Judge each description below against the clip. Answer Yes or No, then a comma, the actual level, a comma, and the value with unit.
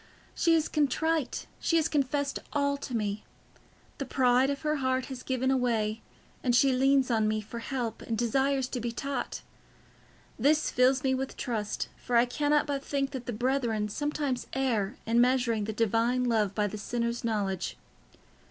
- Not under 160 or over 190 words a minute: Yes, average, 170 wpm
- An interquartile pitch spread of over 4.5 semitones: No, average, 3.3 semitones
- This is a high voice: Yes, very high, 250 Hz